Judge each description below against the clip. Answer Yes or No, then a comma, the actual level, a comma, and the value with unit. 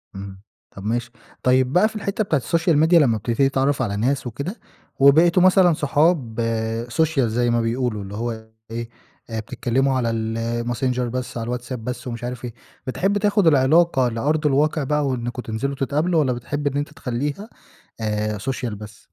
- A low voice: Yes, low, 130 Hz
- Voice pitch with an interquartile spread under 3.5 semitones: No, average, 4.3 semitones